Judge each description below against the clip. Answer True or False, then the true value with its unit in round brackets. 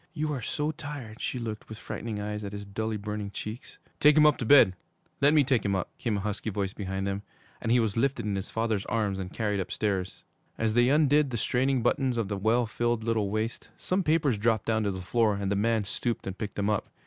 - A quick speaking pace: True (240 wpm)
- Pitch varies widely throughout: False (3.3 semitones)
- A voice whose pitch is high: False (110 Hz)